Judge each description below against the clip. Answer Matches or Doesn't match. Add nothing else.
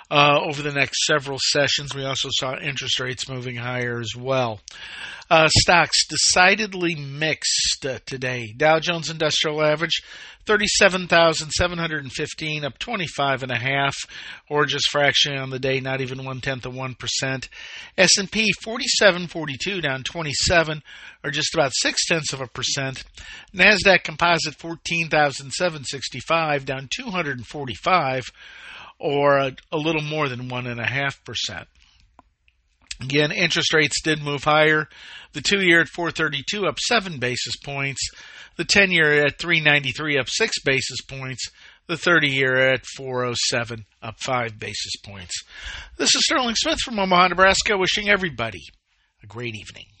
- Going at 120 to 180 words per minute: Matches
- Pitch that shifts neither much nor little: Matches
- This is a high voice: Doesn't match